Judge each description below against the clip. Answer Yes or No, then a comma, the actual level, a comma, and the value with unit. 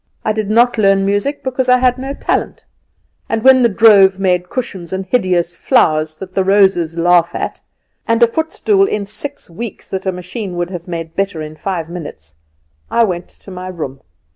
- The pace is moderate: Yes, average, 190 wpm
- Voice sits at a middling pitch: No, high, 195 Hz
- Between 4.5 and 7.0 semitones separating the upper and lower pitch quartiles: Yes, average, 4.8 semitones